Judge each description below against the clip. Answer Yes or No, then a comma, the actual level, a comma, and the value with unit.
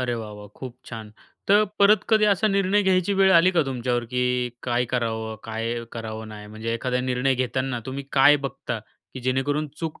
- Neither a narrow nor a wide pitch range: No, wide, 5.9 semitones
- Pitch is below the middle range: Yes, low, 125 Hz